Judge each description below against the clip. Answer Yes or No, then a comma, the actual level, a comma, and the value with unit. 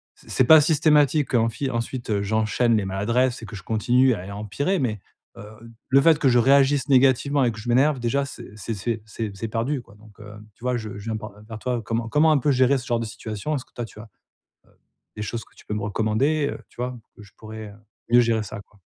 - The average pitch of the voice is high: No, low, 115 Hz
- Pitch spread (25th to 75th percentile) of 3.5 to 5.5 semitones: Yes, average, 3.8 semitones